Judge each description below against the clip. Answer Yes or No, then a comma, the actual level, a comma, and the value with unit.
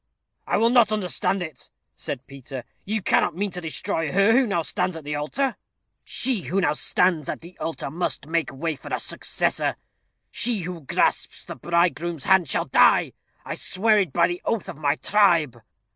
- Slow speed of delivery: No, average, 185 wpm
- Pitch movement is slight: No, average, 4.3 semitones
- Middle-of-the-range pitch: Yes, medium, 175 Hz